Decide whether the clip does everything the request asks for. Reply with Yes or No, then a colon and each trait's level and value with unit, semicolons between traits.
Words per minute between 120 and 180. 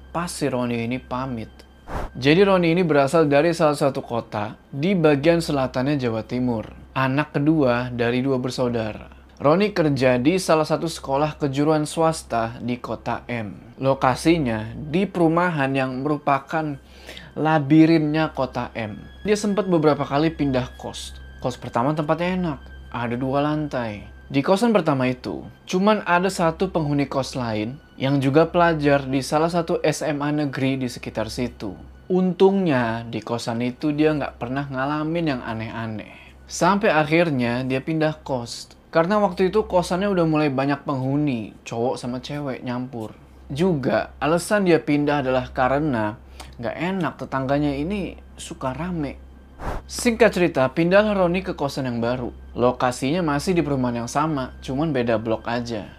Yes: fast, 140 wpm